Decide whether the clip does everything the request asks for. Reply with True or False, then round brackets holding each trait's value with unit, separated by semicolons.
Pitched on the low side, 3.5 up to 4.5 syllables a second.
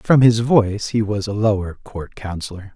False (105 Hz; 4.9 syllables/s)